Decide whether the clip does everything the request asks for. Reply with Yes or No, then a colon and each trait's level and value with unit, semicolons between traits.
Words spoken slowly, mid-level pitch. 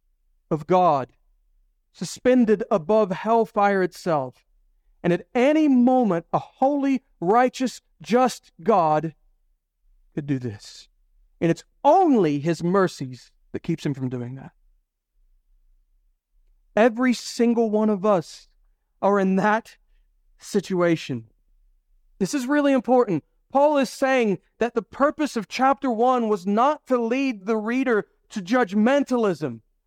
No: slow, 120 wpm; high, 200 Hz